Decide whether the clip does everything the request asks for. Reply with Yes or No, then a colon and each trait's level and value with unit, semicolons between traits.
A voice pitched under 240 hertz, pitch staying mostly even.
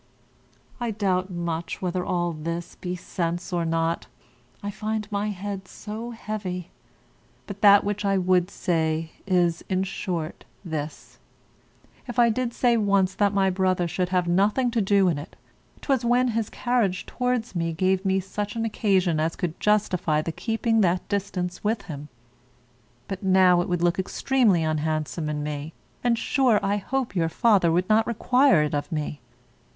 No: high, 190 Hz; average, 3.8 semitones